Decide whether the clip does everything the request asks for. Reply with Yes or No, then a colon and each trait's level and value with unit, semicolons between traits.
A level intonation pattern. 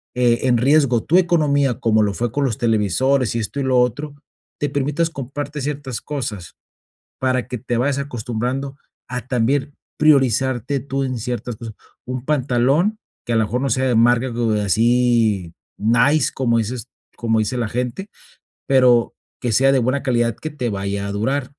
No: average, 3.1 semitones